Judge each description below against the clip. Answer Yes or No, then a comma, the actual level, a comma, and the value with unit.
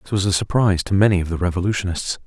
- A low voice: Yes, very low, 95 Hz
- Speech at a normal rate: No, fast, 240 wpm